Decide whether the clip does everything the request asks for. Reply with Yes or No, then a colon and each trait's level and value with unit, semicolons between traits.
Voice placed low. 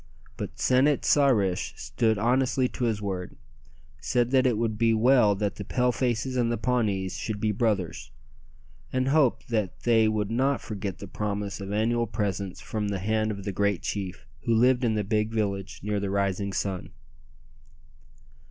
Yes: low, 110 Hz